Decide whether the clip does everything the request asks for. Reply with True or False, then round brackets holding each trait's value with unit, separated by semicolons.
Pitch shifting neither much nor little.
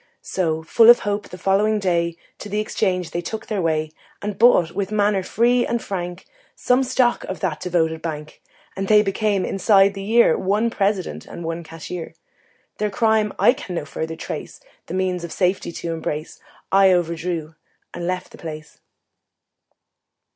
True (3.9 semitones)